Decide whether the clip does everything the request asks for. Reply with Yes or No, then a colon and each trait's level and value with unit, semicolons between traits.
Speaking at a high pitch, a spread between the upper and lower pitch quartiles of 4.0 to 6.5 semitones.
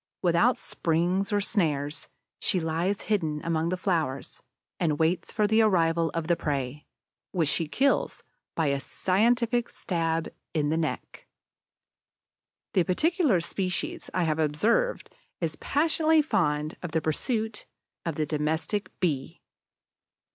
No: medium, 170 Hz; average, 4.9 semitones